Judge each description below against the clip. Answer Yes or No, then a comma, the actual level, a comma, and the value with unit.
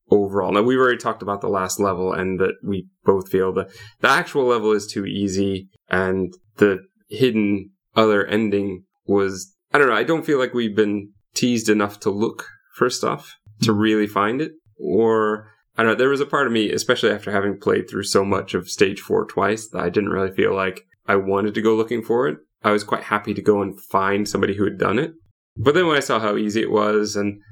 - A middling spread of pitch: No, narrow, 2.0 semitones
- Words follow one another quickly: Yes, fast, 225 wpm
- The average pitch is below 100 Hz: No, low, 105 Hz